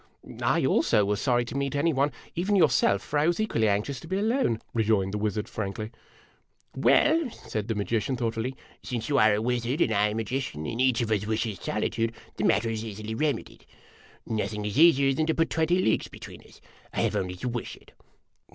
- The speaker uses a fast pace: Yes, fast, 215 wpm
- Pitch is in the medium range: No, low, 115 Hz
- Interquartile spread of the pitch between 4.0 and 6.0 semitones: Yes, average, 5.0 semitones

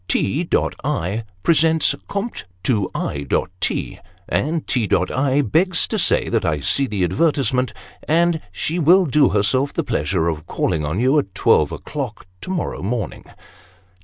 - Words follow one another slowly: No, average, 155 wpm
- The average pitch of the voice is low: Yes, low, 130 Hz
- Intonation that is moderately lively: No, wide, 8.7 semitones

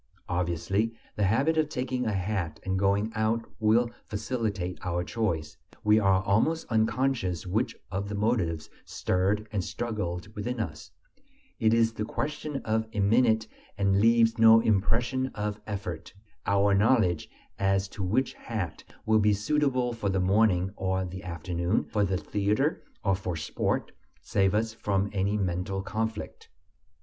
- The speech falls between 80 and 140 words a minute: No, average, 150 wpm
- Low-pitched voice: Yes, low, 105 Hz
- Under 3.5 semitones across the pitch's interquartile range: Yes, average, 3.1 semitones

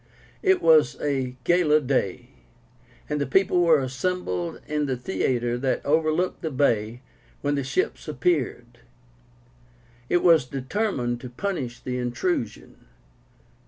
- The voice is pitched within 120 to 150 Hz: Yes, medium, 140 Hz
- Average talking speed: No, slow, 125 wpm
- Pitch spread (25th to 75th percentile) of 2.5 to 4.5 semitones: No, average, 5.3 semitones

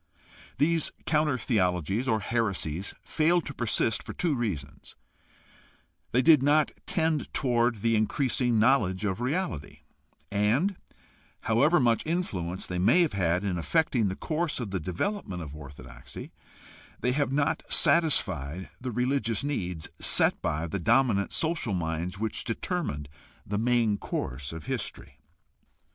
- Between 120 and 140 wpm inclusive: Yes, slow, 135 wpm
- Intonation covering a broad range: Yes, wide, 7.7 semitones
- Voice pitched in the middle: No, low, 115 Hz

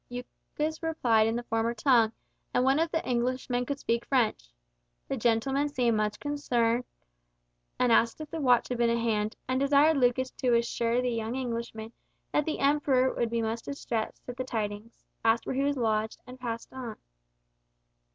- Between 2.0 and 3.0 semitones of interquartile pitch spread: Yes, narrow, 2.6 semitones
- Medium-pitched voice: No, high, 245 Hz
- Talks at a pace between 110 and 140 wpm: No, average, 175 wpm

